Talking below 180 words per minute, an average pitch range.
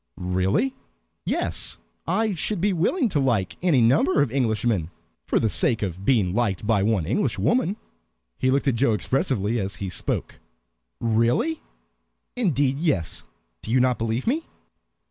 No: average, 145 wpm; wide, 7.4 semitones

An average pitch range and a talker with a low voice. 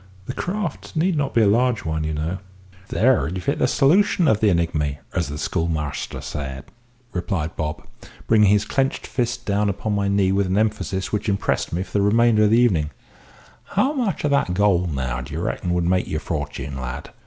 No: wide, 6.2 semitones; low, 100 Hz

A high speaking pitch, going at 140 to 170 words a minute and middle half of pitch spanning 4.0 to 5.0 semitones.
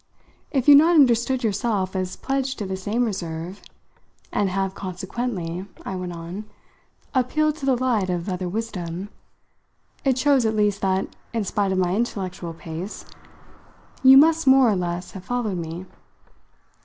No: high, 200 Hz; average, 155 wpm; wide, 5.4 semitones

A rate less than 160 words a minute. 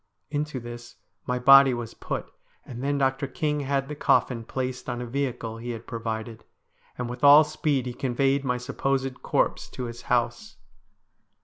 No: average, 170 wpm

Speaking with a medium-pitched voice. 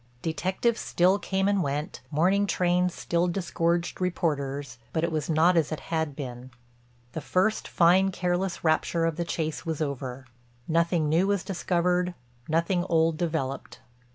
Yes: medium, 170 Hz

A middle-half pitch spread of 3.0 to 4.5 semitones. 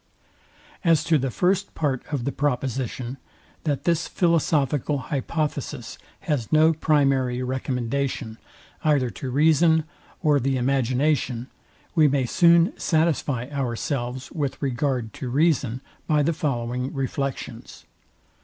Yes: average, 3.4 semitones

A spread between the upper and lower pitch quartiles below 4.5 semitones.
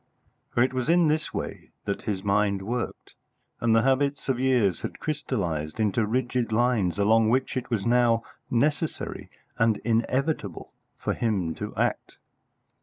Yes: average, 4.0 semitones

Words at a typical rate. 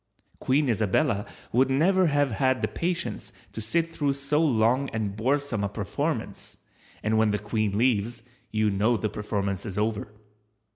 Yes: average, 155 wpm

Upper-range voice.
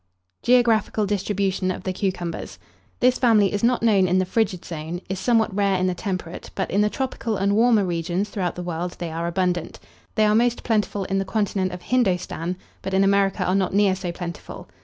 Yes: high, 195 Hz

